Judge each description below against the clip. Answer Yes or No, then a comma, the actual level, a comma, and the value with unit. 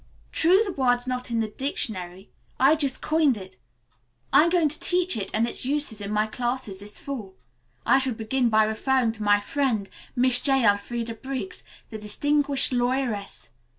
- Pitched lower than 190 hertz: No, high, 245 Hz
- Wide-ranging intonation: No, average, 4.2 semitones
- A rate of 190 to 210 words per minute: No, average, 170 wpm